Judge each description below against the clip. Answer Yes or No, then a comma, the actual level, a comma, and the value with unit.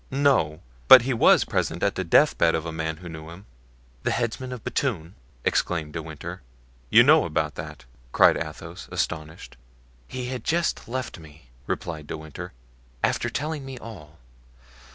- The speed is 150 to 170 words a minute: Yes, average, 160 wpm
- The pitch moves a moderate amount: No, wide, 8.2 semitones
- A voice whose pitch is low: Yes, very low, 85 Hz